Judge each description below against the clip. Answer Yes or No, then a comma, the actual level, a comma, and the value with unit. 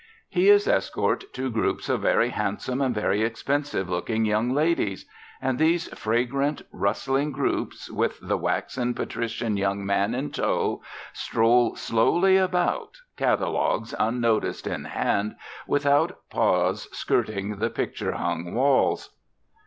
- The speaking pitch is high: No, low, 125 Hz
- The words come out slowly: Yes, slow, 125 wpm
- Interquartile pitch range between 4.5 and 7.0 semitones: Yes, average, 4.9 semitones